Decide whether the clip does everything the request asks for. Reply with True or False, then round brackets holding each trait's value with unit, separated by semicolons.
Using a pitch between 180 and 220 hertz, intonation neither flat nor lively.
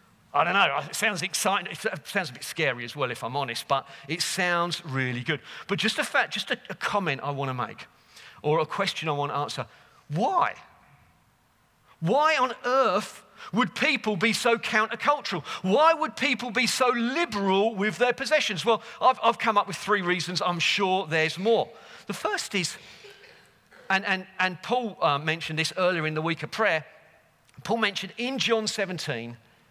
False (190 Hz; 6.7 semitones)